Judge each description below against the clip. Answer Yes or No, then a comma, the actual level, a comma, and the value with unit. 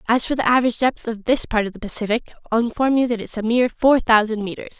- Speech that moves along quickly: Yes, fast, 265 wpm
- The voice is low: No, high, 230 Hz